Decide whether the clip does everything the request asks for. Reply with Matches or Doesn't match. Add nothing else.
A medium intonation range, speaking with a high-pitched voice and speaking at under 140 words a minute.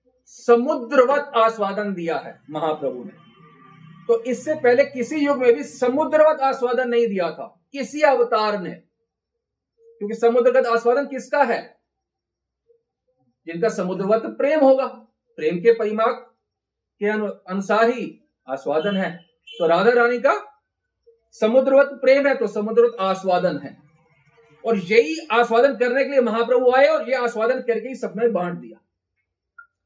Matches